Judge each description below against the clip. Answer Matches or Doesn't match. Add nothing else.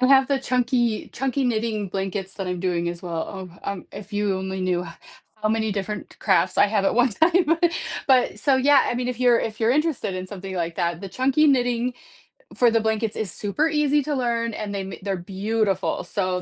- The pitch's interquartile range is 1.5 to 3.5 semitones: Doesn't match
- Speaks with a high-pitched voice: Matches